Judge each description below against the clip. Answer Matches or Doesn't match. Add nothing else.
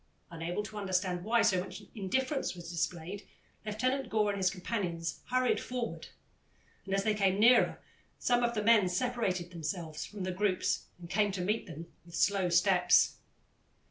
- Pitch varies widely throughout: Doesn't match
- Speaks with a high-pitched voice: Matches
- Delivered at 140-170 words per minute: Matches